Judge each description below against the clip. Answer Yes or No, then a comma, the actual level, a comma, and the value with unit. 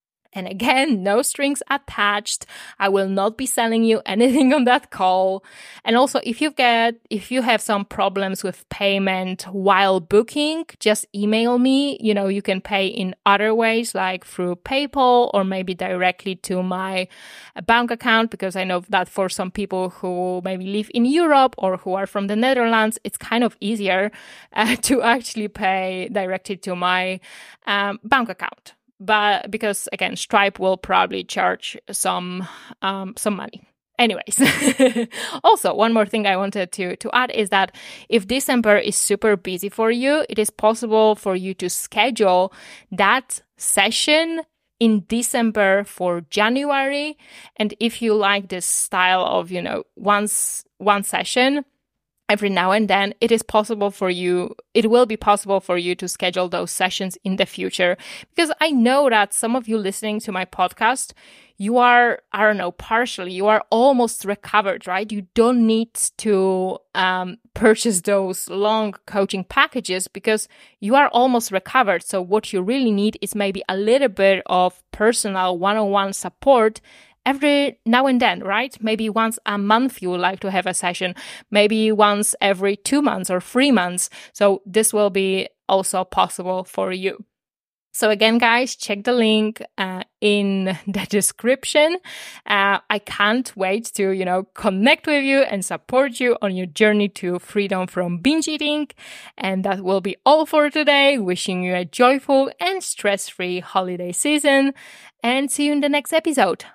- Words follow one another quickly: No, average, 165 wpm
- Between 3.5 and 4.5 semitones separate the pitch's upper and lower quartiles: Yes, average, 4.1 semitones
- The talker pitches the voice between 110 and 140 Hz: No, high, 210 Hz